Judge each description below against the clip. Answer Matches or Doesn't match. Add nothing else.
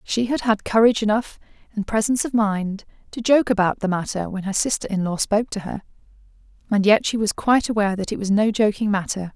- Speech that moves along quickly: Matches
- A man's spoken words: Doesn't match